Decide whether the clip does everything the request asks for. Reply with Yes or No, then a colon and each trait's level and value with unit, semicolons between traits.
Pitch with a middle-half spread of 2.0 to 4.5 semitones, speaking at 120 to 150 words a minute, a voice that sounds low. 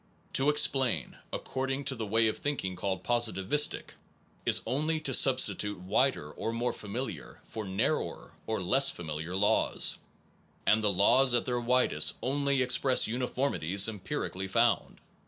No: wide, 5.4 semitones; average, 140 wpm; low, 115 Hz